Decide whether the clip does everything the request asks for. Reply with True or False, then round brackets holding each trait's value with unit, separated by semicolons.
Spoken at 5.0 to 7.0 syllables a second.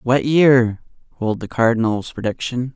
False (4.7 syllables/s)